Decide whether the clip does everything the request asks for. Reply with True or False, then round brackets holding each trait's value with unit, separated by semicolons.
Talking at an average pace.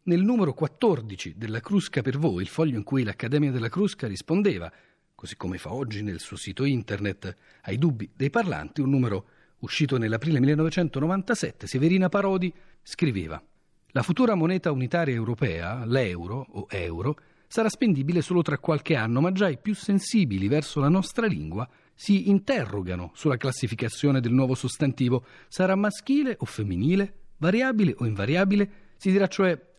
True (150 wpm)